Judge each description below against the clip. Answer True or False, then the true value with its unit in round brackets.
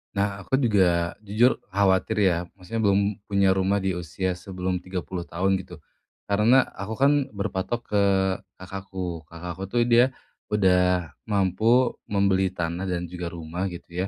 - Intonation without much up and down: True (2.1 semitones)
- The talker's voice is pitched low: True (95 Hz)